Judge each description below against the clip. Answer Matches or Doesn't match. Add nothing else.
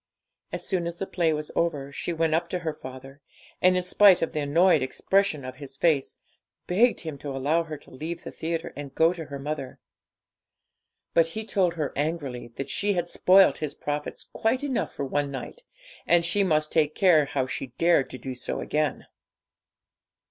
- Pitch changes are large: Doesn't match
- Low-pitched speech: Doesn't match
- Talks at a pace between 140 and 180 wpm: Doesn't match